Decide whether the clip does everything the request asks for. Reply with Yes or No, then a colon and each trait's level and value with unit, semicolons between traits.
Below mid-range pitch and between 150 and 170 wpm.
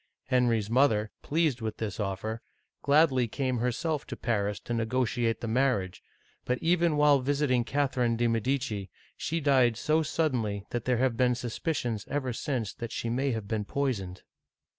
Yes: low, 125 Hz; average, 160 wpm